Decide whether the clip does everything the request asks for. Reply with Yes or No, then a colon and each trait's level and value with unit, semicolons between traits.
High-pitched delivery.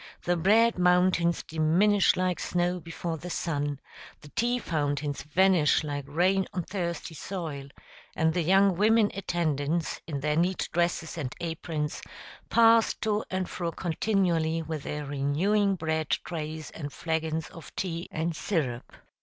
No: medium, 170 Hz